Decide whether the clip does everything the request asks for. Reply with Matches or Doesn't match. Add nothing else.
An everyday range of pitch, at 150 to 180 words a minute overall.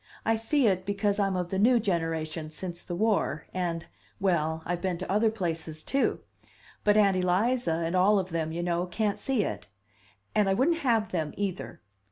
Doesn't match